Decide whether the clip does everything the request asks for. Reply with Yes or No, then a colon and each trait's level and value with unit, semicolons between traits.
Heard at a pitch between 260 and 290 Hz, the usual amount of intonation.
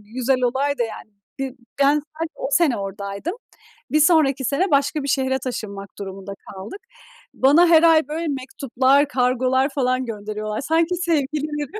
Yes: very high, 270 Hz; average, 3.8 semitones